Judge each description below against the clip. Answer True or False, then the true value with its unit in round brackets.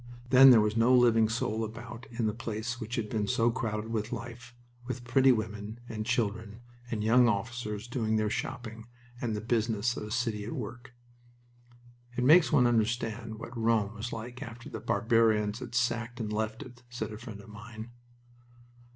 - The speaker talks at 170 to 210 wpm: True (180 wpm)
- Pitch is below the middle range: True (115 Hz)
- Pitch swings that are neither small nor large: False (1.7 semitones)